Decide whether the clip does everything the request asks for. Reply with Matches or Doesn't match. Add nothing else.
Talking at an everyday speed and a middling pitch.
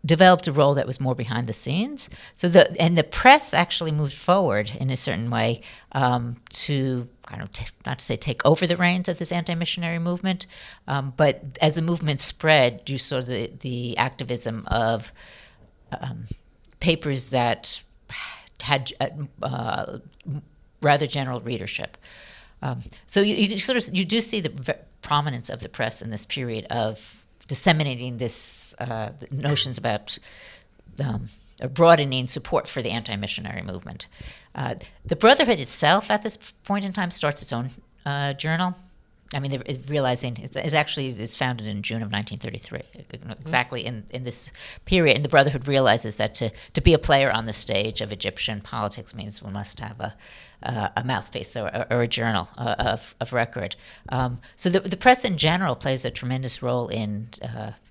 Doesn't match